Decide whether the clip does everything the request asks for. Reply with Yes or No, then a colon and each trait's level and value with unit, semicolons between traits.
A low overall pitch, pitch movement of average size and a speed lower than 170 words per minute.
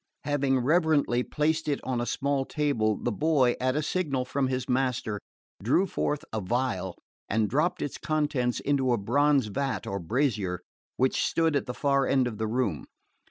No: low, 130 Hz; average, 3.3 semitones; average, 175 wpm